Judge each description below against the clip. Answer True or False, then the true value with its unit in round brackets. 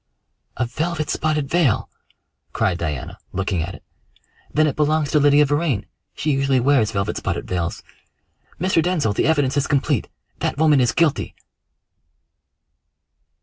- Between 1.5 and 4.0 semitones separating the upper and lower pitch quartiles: False (5.3 semitones)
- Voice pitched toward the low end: False (145 Hz)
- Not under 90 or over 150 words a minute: True (140 wpm)